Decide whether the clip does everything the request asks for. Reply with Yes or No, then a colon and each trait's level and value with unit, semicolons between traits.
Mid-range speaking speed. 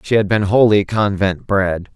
Yes: average, 185 wpm